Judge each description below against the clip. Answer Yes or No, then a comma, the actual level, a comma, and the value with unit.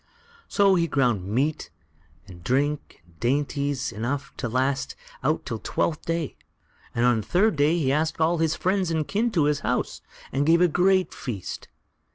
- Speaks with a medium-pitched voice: Yes, medium, 145 Hz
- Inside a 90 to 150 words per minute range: No, average, 175 wpm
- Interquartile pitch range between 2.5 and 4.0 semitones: No, average, 4.7 semitones